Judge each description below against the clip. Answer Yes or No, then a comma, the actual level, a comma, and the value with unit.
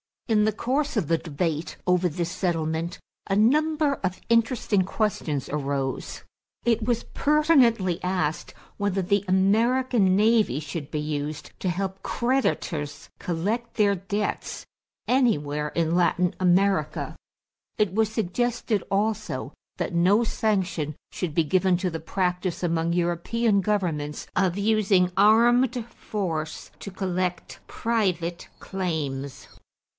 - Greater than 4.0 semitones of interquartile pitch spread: Yes, average, 4.6 semitones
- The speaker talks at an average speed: No, slow, 120 wpm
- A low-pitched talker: No, high, 190 Hz